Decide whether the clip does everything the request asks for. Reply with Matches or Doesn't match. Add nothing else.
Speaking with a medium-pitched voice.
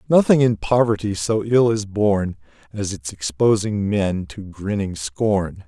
Doesn't match